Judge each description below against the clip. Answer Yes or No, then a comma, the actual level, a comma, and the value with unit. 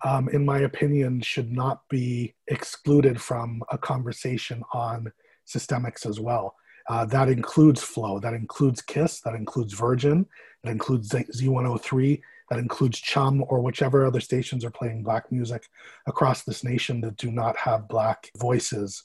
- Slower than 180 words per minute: Yes, average, 150 wpm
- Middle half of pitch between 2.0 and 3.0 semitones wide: Yes, average, 2.7 semitones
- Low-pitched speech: Yes, low, 125 Hz